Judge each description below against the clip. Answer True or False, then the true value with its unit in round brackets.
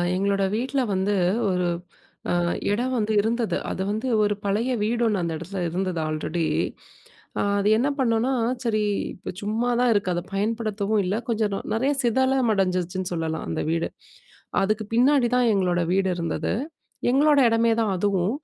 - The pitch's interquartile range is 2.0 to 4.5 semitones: True (4.1 semitones)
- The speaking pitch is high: True (210 Hz)